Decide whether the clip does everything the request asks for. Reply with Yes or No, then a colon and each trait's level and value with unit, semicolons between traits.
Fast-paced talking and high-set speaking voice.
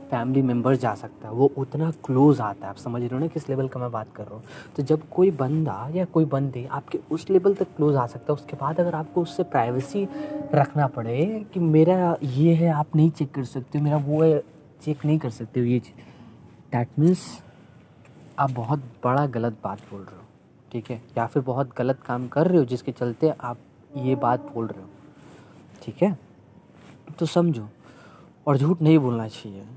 No: fast, 210 wpm; medium, 140 Hz